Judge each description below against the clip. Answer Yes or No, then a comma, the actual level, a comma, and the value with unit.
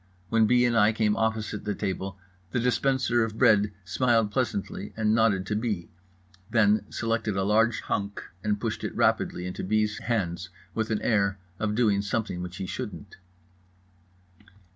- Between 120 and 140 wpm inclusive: No, average, 160 wpm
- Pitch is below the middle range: Yes, low, 105 Hz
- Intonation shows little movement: Yes, narrow, 2.2 semitones